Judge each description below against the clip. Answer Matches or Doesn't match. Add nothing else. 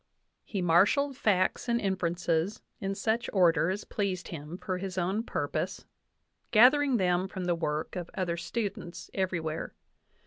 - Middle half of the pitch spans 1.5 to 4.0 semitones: Matches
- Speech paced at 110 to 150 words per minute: Matches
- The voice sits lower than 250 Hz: Matches